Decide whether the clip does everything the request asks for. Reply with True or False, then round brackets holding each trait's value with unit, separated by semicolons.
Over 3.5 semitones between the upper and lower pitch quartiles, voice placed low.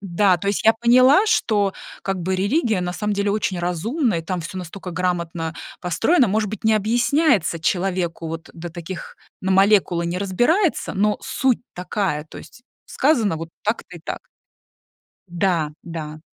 False (4.0 semitones; 190 Hz)